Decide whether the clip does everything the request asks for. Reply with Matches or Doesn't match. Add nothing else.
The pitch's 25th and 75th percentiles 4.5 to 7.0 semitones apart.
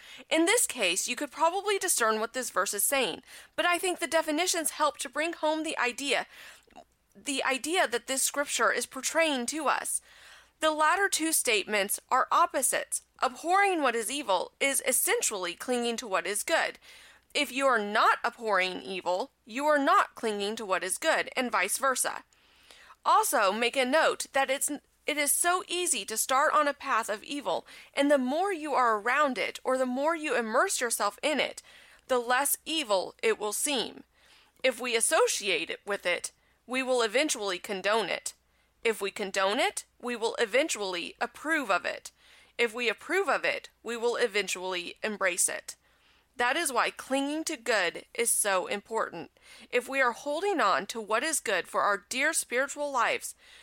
Matches